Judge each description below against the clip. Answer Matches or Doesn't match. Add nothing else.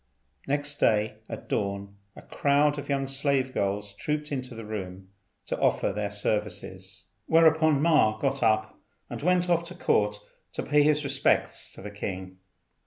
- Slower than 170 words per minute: Matches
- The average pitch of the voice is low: Matches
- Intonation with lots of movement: Matches